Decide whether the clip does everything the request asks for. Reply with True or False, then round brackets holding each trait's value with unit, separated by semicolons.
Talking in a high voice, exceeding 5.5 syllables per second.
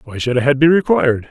False (135 Hz; 6.7 syllables/s)